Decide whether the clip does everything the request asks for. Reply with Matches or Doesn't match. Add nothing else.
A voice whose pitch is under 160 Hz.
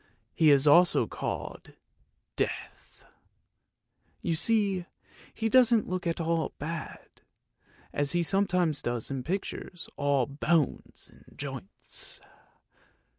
Doesn't match